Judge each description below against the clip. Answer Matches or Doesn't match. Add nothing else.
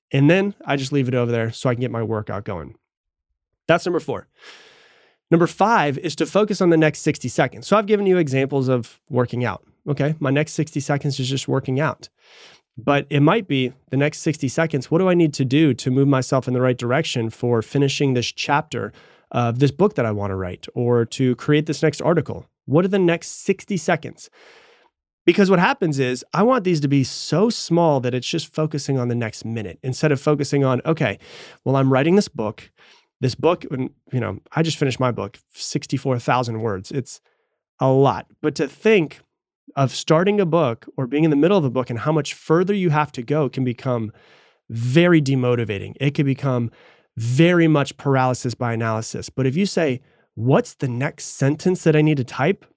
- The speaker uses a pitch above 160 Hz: Doesn't match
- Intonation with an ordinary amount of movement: Matches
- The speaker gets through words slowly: Doesn't match